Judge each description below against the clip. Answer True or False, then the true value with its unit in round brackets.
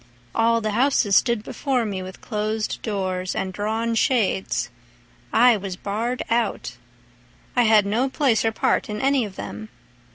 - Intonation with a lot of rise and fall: False (3.5 semitones)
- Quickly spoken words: False (150 wpm)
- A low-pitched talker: False (215 Hz)